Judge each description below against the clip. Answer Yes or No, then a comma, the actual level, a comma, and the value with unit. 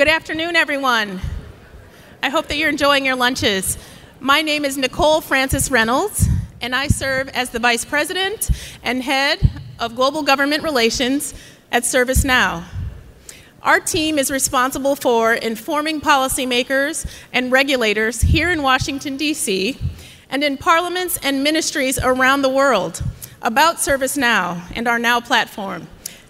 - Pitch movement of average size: Yes, average, 3.3 semitones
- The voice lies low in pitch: No, very high, 275 Hz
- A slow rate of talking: Yes, slow, 130 wpm